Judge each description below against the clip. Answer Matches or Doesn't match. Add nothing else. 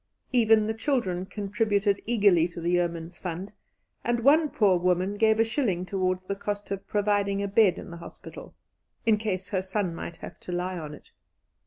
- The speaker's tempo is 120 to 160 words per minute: Doesn't match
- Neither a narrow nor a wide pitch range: Matches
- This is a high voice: Matches